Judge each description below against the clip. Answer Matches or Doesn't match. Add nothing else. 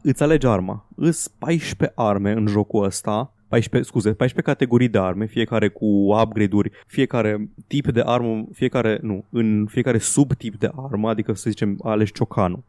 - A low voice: Matches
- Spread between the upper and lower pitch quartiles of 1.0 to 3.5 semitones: Matches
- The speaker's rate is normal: Matches